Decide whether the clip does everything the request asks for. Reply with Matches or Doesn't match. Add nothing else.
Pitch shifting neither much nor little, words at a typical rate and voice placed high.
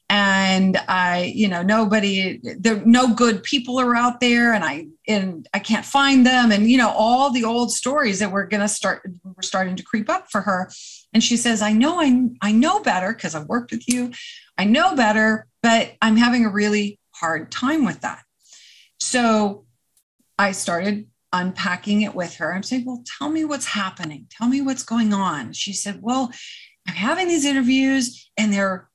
Matches